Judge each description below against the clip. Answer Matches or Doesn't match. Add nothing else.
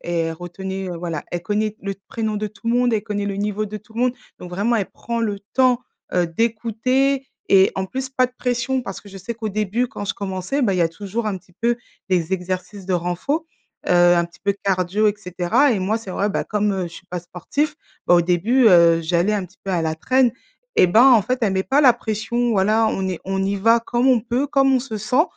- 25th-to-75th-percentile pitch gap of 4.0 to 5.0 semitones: Matches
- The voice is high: Matches